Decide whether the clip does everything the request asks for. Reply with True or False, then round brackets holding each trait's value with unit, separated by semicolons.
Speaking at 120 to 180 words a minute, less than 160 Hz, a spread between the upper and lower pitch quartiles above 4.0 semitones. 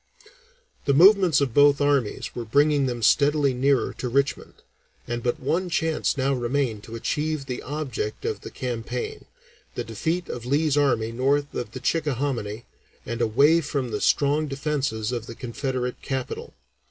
False (155 wpm; 135 Hz; 3.3 semitones)